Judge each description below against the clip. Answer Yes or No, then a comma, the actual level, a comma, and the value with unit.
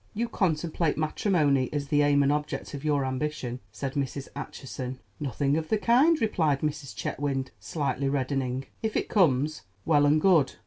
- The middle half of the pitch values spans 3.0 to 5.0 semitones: No, narrow, 2.4 semitones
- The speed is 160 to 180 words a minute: Yes, average, 165 wpm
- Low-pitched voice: No, medium, 145 Hz